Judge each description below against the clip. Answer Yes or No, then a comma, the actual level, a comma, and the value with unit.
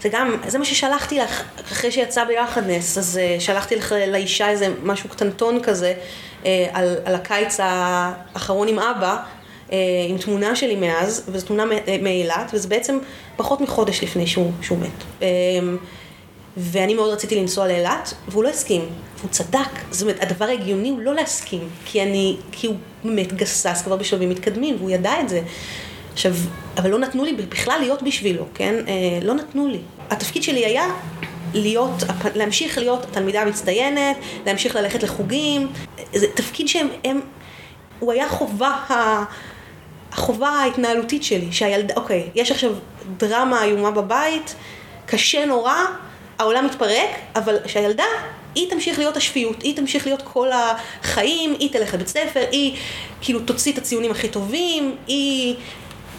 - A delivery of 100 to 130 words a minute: No, average, 145 wpm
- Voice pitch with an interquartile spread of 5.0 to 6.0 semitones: Yes, average, 5.3 semitones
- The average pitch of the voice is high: Yes, high, 215 Hz